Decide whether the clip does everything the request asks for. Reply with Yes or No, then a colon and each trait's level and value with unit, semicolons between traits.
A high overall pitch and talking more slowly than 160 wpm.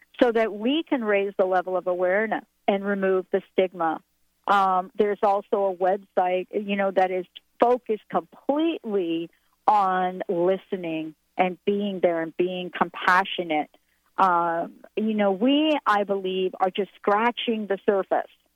Yes: high, 195 Hz; average, 140 wpm